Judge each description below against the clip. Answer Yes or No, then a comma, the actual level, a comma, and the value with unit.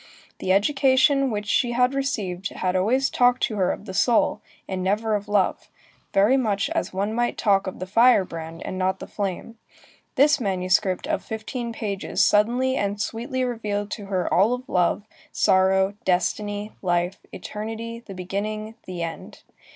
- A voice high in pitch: Yes, high, 205 Hz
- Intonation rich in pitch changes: No, average, 4.1 semitones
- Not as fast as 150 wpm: No, average, 165 wpm